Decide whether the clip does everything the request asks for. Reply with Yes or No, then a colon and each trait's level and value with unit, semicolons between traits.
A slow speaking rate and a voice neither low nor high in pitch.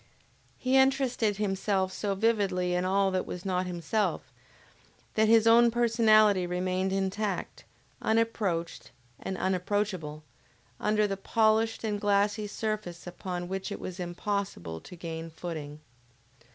No: slow, 125 wpm; high, 195 Hz